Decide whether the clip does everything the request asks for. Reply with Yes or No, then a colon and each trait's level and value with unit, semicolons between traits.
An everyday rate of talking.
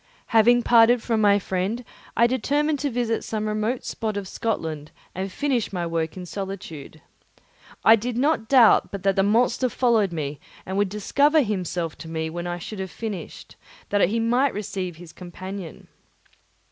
Yes: average, 170 wpm